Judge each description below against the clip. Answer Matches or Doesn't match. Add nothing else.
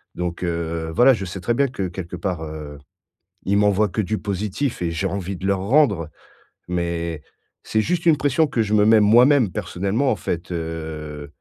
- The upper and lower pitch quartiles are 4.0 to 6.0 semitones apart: Matches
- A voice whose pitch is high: Doesn't match